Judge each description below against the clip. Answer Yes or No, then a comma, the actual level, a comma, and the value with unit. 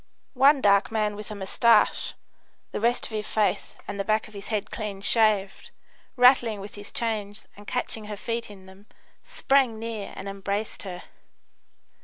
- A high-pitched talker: Yes, high, 210 Hz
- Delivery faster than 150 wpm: Yes, average, 170 wpm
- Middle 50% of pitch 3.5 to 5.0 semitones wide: No, narrow, 2.4 semitones